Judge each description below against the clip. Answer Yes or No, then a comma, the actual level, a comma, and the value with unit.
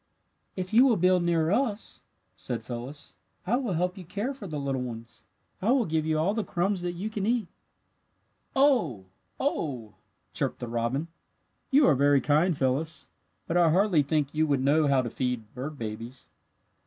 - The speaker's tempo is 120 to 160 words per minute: No, average, 180 wpm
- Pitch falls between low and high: Yes, medium, 160 Hz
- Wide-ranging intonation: Yes, wide, 6.6 semitones